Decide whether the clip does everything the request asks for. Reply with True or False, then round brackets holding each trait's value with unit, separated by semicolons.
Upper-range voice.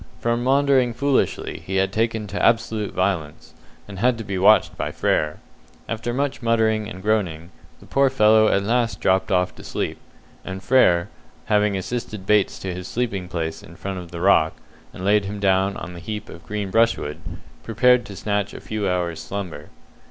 False (100 Hz)